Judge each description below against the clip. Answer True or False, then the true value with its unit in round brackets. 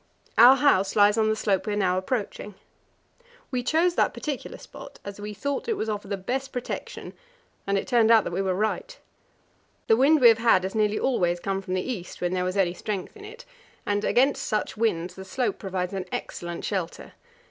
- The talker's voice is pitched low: False (210 Hz)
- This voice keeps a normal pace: False (210 wpm)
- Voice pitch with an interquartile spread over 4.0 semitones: True (4.6 semitones)